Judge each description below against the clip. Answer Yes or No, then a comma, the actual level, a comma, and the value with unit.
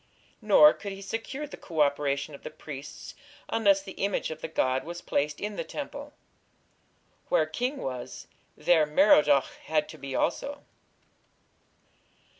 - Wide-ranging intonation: Yes, wide, 6.5 semitones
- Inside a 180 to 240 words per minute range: No, average, 145 wpm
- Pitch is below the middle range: No, medium, 165 Hz